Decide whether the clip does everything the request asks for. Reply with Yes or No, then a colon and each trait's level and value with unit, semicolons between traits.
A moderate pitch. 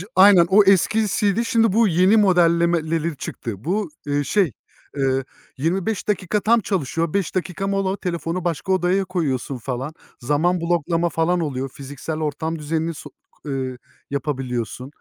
Yes: medium, 170 Hz